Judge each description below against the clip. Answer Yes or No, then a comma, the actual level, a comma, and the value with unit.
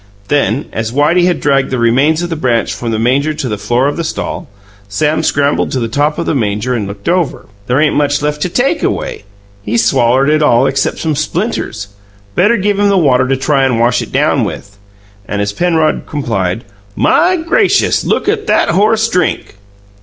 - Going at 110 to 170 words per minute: No, average, 200 wpm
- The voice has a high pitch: No, medium, 145 Hz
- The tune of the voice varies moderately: No, wide, 6.1 semitones